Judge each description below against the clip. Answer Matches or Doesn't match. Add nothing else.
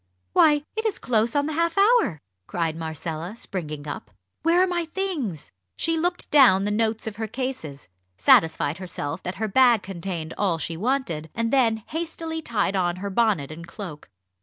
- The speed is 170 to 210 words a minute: Matches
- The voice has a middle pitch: Doesn't match